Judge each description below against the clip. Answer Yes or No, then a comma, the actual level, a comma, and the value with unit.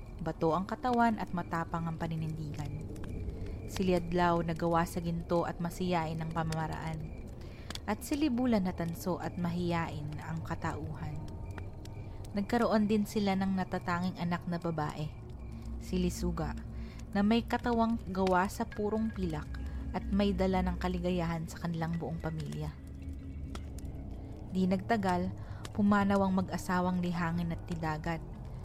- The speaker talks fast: No, average, 120 wpm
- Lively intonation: Yes, wide, 6.8 semitones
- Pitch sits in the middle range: Yes, medium, 170 Hz